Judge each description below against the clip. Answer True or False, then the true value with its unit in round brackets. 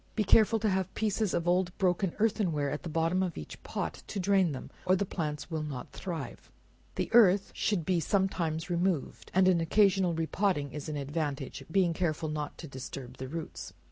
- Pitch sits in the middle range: True (170 Hz)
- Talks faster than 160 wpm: True (200 wpm)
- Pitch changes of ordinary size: True (3.9 semitones)